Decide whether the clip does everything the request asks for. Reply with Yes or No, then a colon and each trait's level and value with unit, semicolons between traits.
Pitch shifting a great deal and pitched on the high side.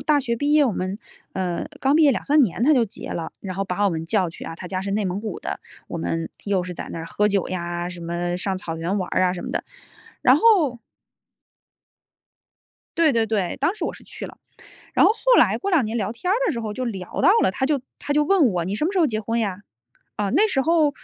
Yes: wide, 7.9 semitones; high, 210 Hz